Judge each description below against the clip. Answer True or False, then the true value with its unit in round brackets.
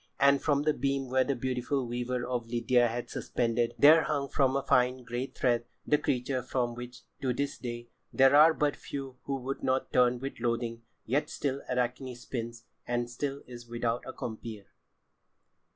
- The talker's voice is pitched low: True (125 Hz)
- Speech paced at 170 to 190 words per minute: True (180 wpm)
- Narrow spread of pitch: True (2.3 semitones)